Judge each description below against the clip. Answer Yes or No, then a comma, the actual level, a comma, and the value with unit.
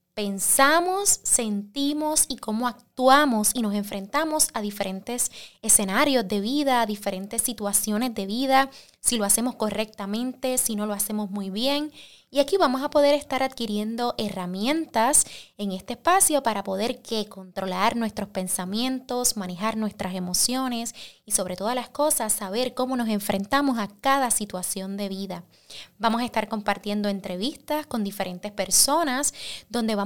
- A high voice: Yes, high, 225 Hz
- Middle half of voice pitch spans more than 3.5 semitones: Yes, average, 4.4 semitones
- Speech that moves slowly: No, average, 145 wpm